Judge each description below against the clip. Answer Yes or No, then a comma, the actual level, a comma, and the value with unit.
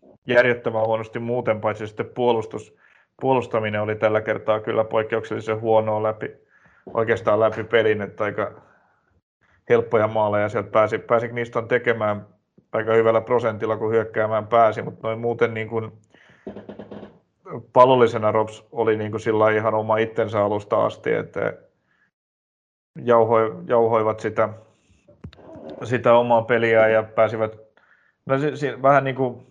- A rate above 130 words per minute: No, average, 120 wpm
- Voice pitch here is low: Yes, low, 110 Hz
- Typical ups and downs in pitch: No, narrow, 1.5 semitones